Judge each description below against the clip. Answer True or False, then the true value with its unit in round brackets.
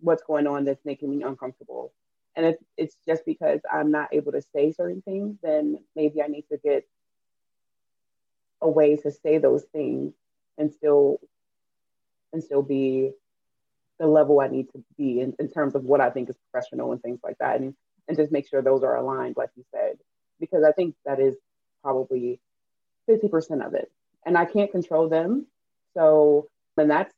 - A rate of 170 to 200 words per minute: True (185 wpm)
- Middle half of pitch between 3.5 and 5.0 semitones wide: False (3.0 semitones)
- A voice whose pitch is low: False (150 Hz)